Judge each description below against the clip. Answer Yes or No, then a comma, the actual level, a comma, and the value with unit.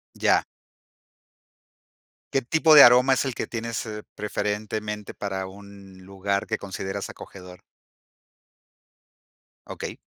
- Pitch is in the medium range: No, low, 105 Hz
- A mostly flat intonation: No, average, 3.1 semitones